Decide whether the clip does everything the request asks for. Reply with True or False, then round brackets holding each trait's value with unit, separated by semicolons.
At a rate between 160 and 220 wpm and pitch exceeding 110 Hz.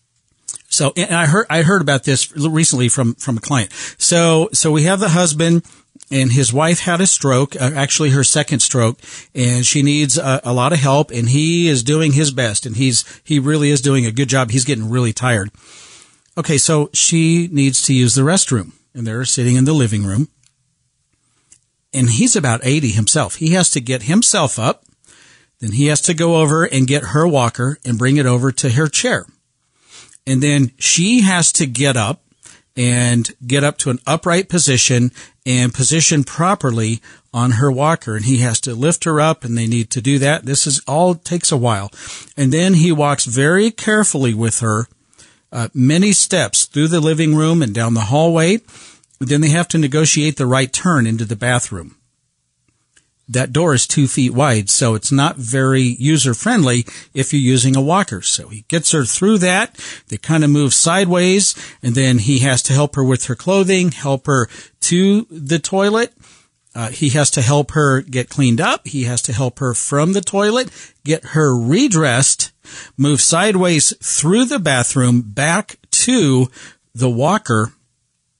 True (185 wpm; 140 Hz)